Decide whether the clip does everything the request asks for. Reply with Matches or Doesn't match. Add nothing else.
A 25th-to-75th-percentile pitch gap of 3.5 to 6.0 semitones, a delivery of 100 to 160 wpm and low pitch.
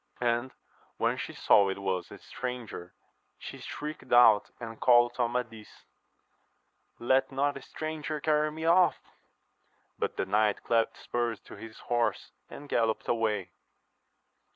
Matches